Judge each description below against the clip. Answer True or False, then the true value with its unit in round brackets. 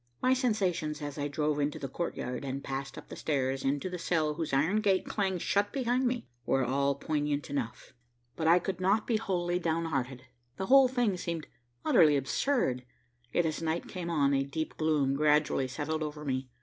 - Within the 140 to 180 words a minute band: False (190 wpm)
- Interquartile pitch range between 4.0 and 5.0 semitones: True (4.7 semitones)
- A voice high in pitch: False (155 Hz)